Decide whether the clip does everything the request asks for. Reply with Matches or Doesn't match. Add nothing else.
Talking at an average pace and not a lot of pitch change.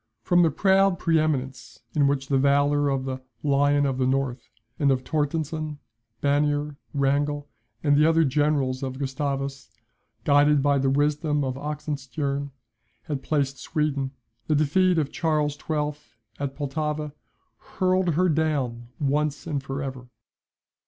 Matches